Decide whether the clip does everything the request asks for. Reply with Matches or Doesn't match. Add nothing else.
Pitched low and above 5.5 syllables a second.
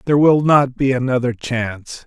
Doesn't match